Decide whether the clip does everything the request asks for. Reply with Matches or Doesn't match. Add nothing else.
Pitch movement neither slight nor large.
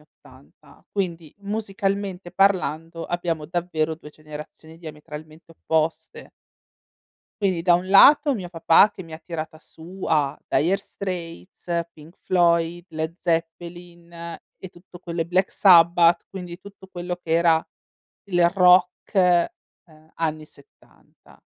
Doesn't match